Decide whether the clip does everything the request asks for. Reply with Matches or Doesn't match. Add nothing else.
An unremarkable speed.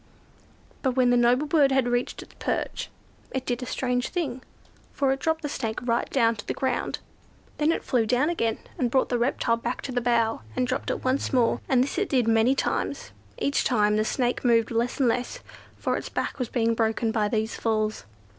Doesn't match